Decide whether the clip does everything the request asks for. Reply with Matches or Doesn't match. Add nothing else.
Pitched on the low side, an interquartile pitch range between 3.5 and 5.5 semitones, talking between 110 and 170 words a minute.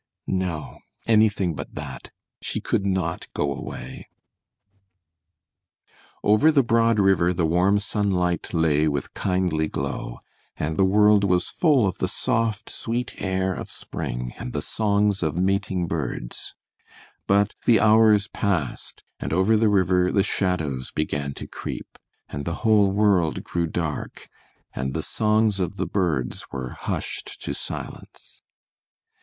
Matches